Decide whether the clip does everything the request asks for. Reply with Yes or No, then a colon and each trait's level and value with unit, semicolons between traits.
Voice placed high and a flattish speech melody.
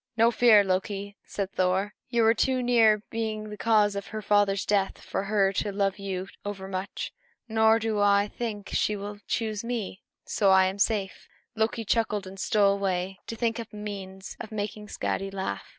Yes: high, 205 Hz; narrow, 2.1 semitones